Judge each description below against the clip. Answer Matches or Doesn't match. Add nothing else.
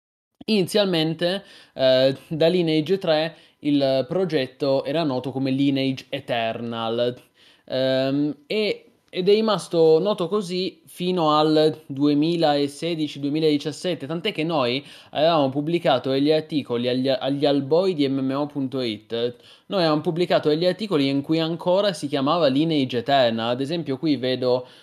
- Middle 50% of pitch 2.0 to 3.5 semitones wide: Doesn't match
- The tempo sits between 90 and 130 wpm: Matches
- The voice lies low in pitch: Doesn't match